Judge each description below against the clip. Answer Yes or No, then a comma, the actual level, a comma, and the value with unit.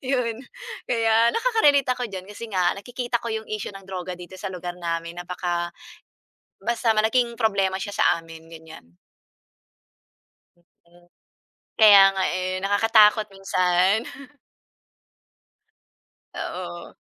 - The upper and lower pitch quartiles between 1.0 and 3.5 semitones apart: No, average, 4.1 semitones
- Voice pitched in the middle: No, high, 195 Hz